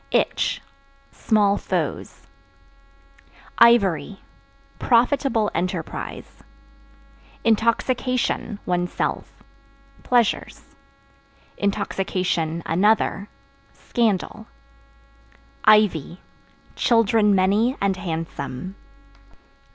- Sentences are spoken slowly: Yes, slow, 50 wpm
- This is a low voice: No, high, 205 Hz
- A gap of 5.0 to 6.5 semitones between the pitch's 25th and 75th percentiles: No, average, 3.8 semitones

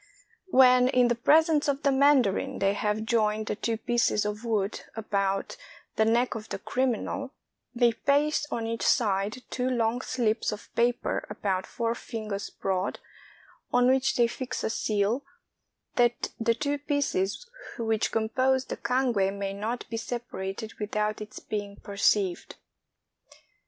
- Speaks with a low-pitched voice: No, high, 230 Hz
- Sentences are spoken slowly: No, average, 145 wpm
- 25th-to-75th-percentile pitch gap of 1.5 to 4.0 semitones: Yes, average, 3.3 semitones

